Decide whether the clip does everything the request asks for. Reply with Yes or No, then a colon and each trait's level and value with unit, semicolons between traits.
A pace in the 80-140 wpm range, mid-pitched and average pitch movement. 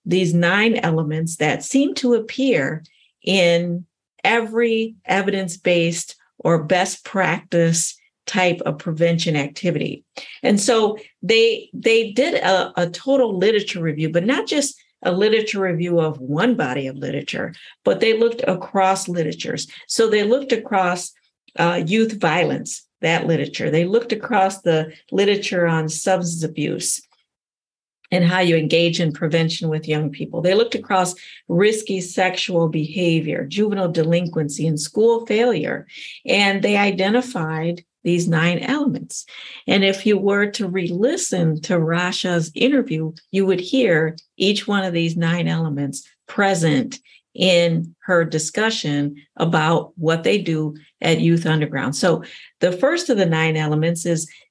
Yes: slow, 135 wpm; medium, 180 Hz; average, 4.5 semitones